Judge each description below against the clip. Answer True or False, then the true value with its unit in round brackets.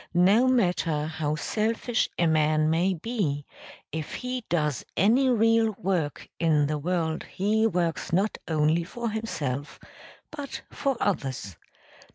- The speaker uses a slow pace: True (130 wpm)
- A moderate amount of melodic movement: False (6.3 semitones)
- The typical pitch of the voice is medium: True (175 Hz)